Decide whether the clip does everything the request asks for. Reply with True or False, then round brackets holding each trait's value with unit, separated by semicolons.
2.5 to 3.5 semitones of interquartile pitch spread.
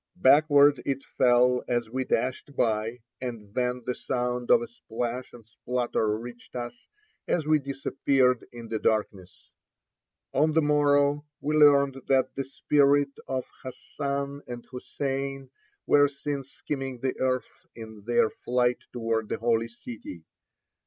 True (2.8 semitones)